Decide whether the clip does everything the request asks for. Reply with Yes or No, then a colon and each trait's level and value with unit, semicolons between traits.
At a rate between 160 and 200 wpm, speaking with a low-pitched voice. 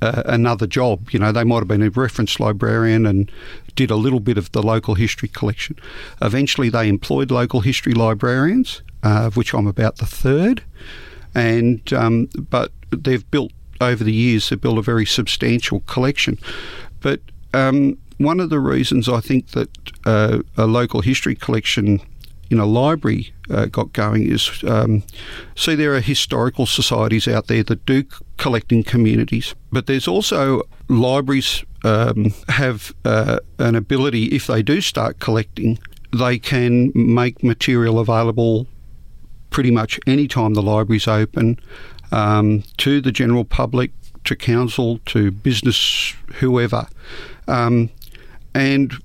No: average, 150 wpm; low, 120 Hz